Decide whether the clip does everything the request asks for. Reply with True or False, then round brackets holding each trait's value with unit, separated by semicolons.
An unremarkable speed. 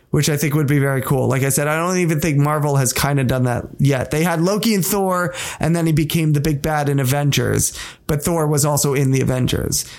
False (250 wpm)